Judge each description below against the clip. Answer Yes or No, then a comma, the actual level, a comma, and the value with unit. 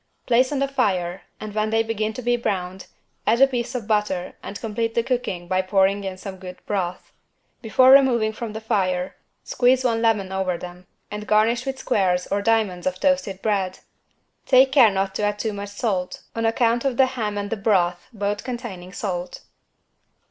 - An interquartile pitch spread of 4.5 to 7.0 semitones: No, average, 3.8 semitones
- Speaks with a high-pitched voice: Yes, high, 210 Hz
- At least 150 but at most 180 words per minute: No, average, 190 wpm